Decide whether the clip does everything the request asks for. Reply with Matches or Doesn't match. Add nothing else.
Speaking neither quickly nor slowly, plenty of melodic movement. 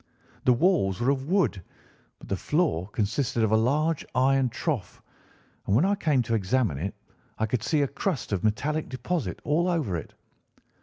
Matches